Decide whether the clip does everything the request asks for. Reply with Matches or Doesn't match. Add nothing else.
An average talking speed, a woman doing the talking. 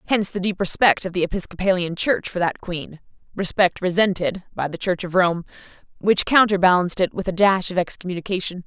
Matches